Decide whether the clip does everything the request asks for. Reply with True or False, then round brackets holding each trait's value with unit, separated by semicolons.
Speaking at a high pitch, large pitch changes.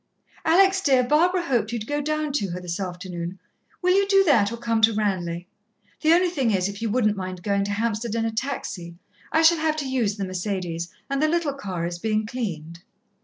True (220 Hz; 7.8 semitones)